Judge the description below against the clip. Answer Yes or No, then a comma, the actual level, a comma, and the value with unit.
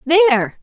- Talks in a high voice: Yes, very high, 295 Hz